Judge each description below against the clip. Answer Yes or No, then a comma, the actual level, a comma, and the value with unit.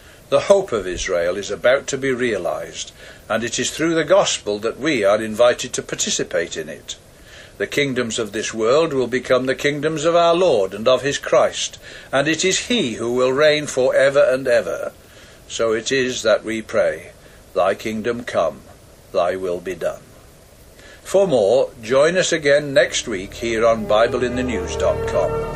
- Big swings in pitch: No, average, 5.0 semitones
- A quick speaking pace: No, average, 170 wpm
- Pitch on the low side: Yes, low, 130 Hz